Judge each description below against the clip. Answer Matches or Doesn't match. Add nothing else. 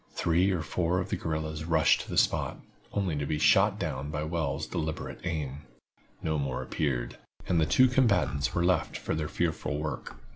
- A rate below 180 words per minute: Doesn't match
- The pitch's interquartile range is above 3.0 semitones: Doesn't match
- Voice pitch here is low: Matches